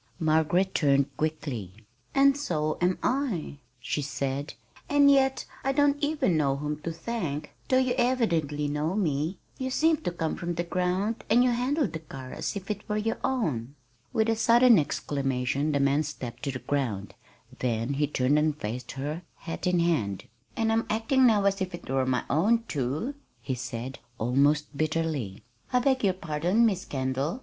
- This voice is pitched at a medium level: Yes, medium, 160 Hz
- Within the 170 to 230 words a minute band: Yes, average, 175 wpm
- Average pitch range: No, wide, 8.2 semitones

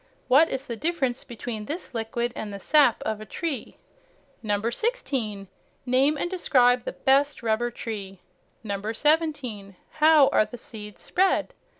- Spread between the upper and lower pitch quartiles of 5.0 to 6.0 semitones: Yes, wide, 5.4 semitones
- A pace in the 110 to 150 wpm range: Yes, slow, 135 wpm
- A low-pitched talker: No, high, 245 Hz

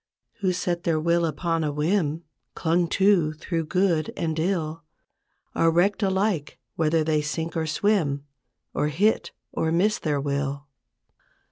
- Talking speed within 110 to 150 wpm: Yes, average, 140 wpm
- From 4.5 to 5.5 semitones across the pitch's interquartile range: No, average, 2.8 semitones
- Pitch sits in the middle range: Yes, medium, 165 Hz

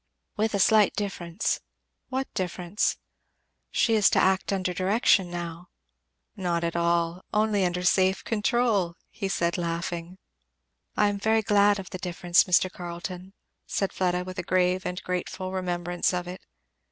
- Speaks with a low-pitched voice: No, medium, 185 Hz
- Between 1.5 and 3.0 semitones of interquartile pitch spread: Yes, narrow, 2.4 semitones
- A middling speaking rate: Yes, average, 150 wpm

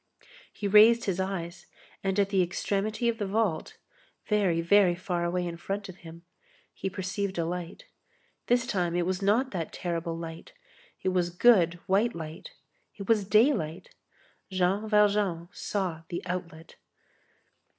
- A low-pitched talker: No, high, 190 Hz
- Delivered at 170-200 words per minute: No, average, 150 wpm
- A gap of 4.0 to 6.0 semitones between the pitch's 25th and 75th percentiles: No, average, 3.1 semitones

